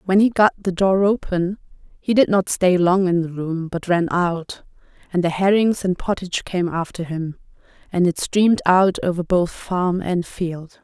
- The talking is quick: No, average, 190 wpm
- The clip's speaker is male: No, female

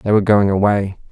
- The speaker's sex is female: No, male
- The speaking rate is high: Yes, fast, 215 wpm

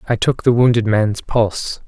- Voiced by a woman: No, male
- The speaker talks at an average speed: Yes, average, 190 wpm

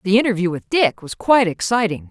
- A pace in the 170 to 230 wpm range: Yes, average, 200 wpm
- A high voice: Yes, high, 200 Hz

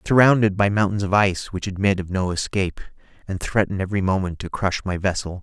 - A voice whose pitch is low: Yes, very low, 95 Hz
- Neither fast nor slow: No, fast, 220 wpm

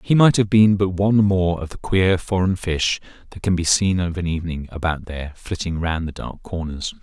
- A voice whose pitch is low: Yes, very low, 90 Hz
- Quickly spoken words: Yes, fast, 220 wpm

